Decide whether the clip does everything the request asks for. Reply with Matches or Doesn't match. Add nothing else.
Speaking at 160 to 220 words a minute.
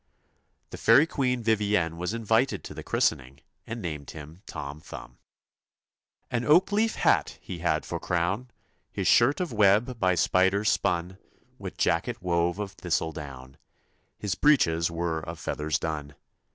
Doesn't match